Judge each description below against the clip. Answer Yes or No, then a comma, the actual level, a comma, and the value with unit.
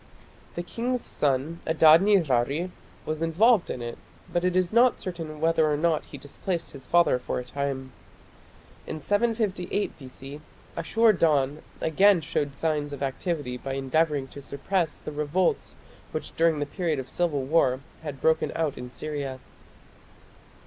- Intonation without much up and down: No, average, 3.9 semitones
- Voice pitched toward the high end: No, medium, 155 Hz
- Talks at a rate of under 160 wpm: Yes, average, 150 wpm